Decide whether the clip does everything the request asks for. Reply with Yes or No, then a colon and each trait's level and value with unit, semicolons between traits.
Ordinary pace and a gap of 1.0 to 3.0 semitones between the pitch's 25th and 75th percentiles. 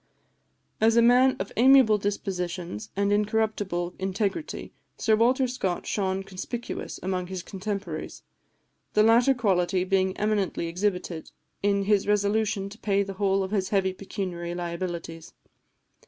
No: slow, 130 wpm; narrow, 2.6 semitones